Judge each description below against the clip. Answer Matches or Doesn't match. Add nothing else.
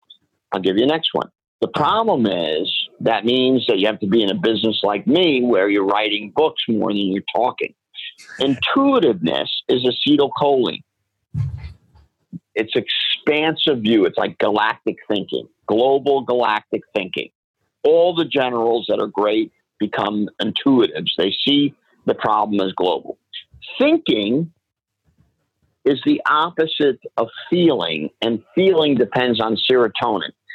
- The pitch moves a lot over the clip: Matches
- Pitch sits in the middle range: Doesn't match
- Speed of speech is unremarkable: Doesn't match